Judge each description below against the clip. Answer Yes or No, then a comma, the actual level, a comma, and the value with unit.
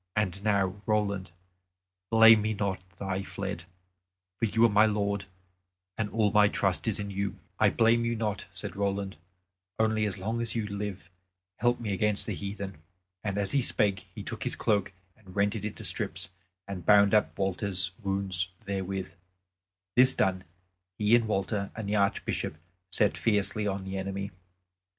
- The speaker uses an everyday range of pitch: No, narrow, 1.8 semitones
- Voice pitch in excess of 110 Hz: No, low, 100 Hz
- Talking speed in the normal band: Yes, average, 170 wpm